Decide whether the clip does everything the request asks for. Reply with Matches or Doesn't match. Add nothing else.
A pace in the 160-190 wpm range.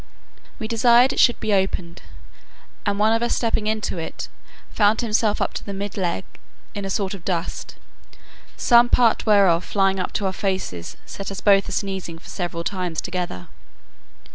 Matches